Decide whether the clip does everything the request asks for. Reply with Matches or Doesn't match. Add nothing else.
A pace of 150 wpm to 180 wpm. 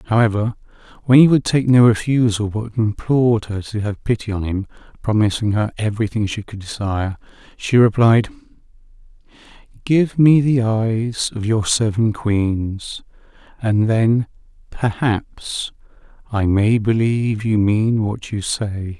Doesn't match